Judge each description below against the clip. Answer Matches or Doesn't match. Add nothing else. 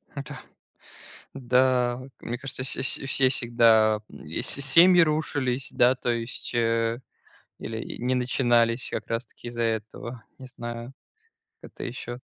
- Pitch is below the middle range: Matches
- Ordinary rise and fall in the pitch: Doesn't match